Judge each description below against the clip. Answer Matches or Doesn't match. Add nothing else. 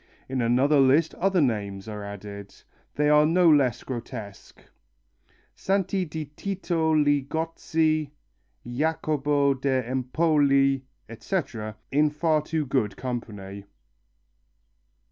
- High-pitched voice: Doesn't match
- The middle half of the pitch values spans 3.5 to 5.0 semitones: Matches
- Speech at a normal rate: Doesn't match